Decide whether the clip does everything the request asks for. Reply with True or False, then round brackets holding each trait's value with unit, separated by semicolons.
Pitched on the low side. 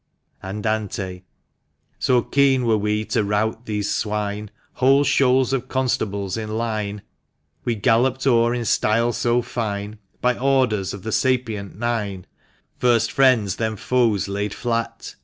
True (110 Hz)